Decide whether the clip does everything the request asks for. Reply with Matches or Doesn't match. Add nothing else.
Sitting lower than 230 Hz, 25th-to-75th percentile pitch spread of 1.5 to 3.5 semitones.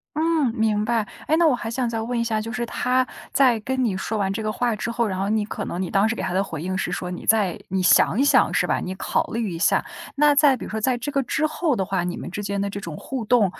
Doesn't match